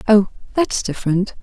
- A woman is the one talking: Yes, female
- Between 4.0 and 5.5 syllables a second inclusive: Yes, 5.1 syllables/s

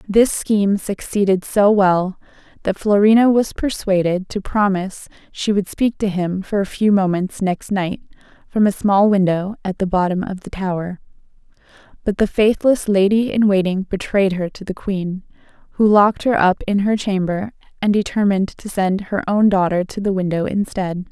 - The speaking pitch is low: No, high, 195 Hz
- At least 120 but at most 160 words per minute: No, average, 175 wpm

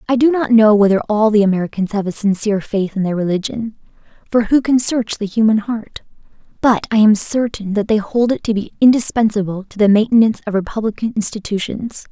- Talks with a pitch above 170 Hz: Yes, high, 215 Hz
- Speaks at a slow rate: No, average, 195 wpm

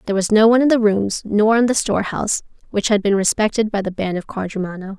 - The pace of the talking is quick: Yes, fast, 240 wpm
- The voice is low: No, high, 205 Hz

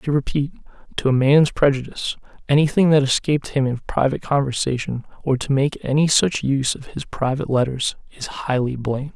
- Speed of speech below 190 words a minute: Yes, average, 170 wpm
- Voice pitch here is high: No, low, 135 Hz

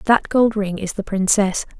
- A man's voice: No, female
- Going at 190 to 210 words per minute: Yes, average, 200 wpm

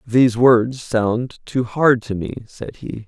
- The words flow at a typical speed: Yes, average, 175 wpm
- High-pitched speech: No, low, 120 Hz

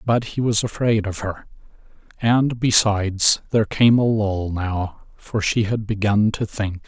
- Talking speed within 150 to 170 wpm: Yes, average, 165 wpm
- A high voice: No, low, 105 Hz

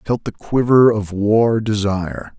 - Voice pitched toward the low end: Yes, low, 110 Hz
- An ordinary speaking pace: Yes, average, 175 wpm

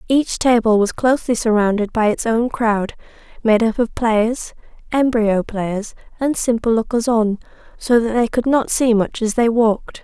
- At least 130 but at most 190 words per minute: Yes, average, 175 wpm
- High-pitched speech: Yes, high, 230 Hz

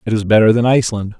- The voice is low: Yes, low, 110 Hz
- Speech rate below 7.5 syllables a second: No, 7.6 syllables/s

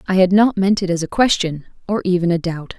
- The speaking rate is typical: No, fast, 260 wpm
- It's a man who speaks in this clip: No, female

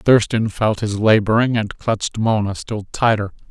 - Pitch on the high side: No, low, 110 Hz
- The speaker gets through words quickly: No, average, 155 wpm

